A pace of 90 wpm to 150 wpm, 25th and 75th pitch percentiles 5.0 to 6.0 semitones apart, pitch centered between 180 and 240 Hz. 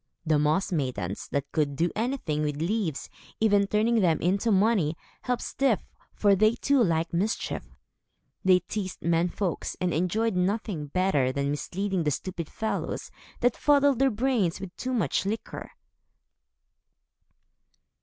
Yes: average, 140 wpm; wide, 5.4 semitones; high, 190 Hz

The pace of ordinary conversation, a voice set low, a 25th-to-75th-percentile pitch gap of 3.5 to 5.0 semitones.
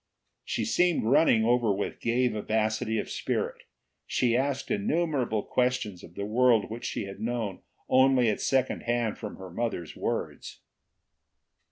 No: average, 145 wpm; low, 120 Hz; average, 3.0 semitones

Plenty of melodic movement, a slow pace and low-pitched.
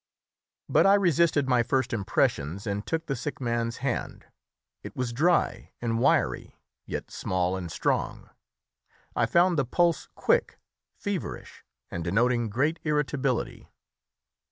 Yes: wide, 5.9 semitones; slow, 130 wpm; low, 125 Hz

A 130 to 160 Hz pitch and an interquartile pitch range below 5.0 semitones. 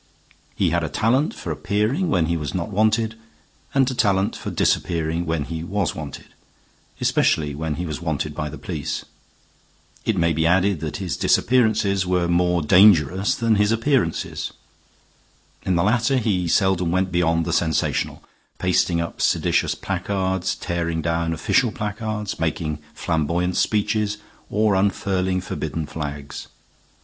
No: very low, 90 Hz; average, 4.2 semitones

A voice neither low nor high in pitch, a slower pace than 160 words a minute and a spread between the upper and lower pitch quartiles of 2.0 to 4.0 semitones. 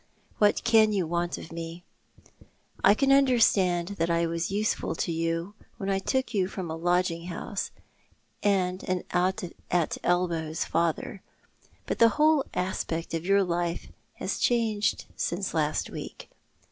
Yes: medium, 180 Hz; average, 150 wpm; average, 3.5 semitones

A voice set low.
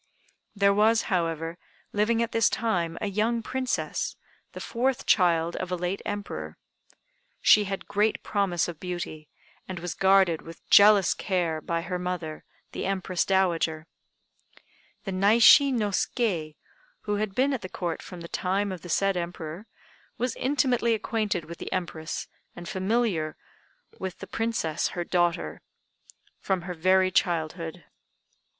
No: medium, 185 Hz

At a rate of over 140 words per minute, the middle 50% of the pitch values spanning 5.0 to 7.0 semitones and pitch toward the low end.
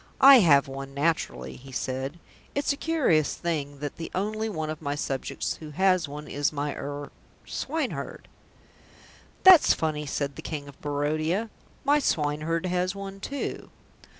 No: average, 150 wpm; average, 5.3 semitones; medium, 155 Hz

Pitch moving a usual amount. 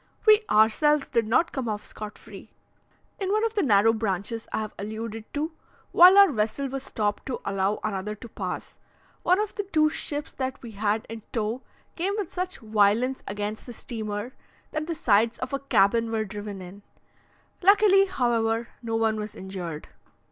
No: wide, 6.0 semitones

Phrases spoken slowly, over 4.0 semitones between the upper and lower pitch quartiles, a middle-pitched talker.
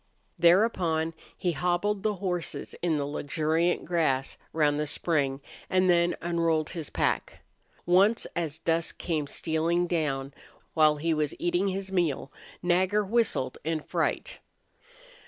No: slow, 130 wpm; average, 2.7 semitones; medium, 170 Hz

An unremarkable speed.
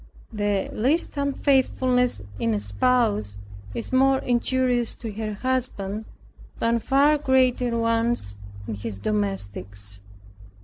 No: slow, 105 wpm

